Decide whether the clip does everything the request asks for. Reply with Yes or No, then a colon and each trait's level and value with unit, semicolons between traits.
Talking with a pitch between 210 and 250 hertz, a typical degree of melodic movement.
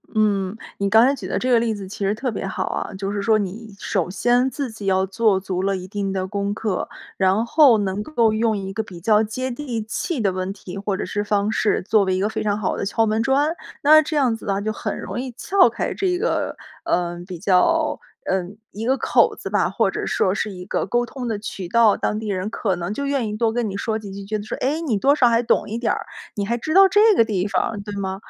Yes: high, 215 Hz; average, 3.5 semitones